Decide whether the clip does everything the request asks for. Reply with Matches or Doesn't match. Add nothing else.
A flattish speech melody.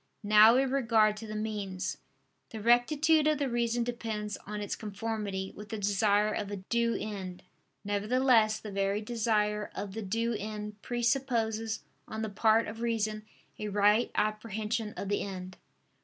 Matches